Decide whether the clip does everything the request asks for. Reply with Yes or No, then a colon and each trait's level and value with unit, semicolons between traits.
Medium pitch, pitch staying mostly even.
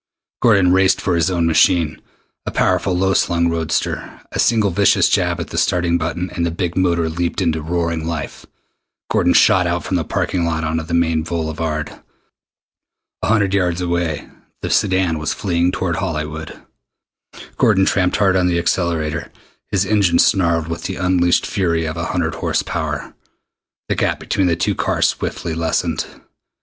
No: very low, 85 Hz; narrow, 2.2 semitones